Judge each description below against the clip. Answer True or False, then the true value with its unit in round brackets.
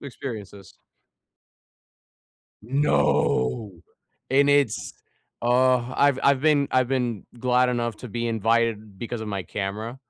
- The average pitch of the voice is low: True (120 Hz)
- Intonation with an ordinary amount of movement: True (3.2 semitones)